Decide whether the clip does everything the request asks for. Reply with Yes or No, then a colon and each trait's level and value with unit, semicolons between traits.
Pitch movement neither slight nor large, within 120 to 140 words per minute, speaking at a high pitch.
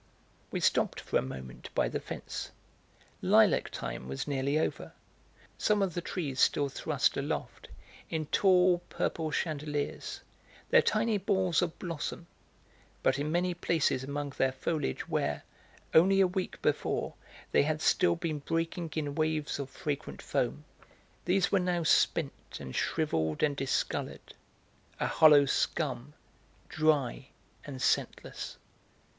No: average, 3.8 semitones; slow, 135 wpm; medium, 155 Hz